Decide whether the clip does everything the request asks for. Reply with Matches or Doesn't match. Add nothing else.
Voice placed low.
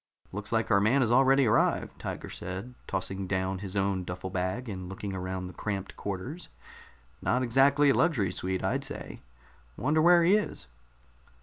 Matches